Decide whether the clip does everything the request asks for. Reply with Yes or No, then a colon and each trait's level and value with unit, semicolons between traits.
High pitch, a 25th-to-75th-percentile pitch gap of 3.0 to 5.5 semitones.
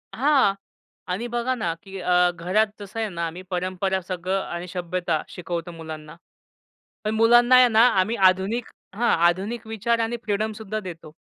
Yes: high, 195 Hz; average, 4.1 semitones